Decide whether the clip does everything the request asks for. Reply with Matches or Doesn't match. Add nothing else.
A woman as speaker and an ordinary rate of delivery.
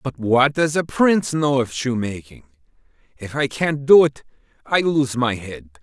Doesn't match